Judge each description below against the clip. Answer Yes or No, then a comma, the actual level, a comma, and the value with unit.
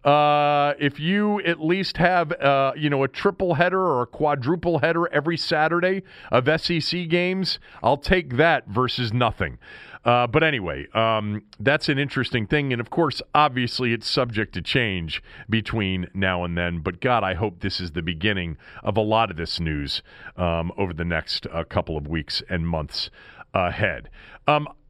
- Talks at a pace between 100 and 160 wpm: No, average, 175 wpm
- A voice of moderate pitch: No, low, 125 Hz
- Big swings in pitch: Yes, wide, 8.8 semitones